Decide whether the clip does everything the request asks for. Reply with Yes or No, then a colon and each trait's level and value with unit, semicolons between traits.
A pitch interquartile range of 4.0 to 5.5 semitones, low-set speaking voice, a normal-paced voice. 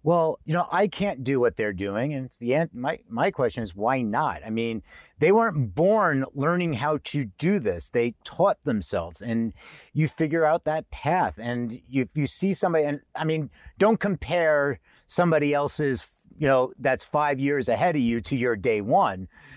No: average, 4.5 semitones; medium, 145 Hz; average, 195 wpm